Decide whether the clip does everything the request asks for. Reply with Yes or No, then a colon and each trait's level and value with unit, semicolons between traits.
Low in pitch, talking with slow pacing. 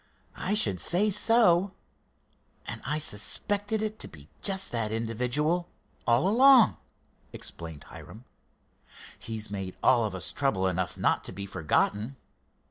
Yes: low, 120 Hz; slow, 130 wpm